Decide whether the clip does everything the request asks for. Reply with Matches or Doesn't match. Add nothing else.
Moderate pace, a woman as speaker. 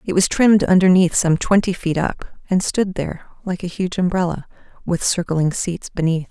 Matches